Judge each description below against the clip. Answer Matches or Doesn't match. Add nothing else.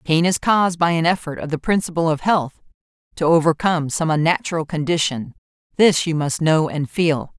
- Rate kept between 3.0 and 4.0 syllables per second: Doesn't match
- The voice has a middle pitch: Matches